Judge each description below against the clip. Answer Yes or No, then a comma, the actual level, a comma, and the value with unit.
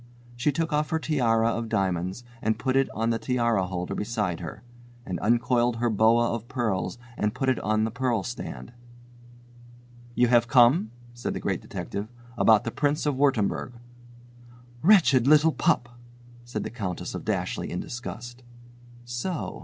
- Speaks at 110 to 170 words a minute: Yes, average, 160 wpm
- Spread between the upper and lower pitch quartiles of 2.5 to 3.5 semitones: Yes, average, 3.0 semitones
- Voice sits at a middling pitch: No, low, 120 Hz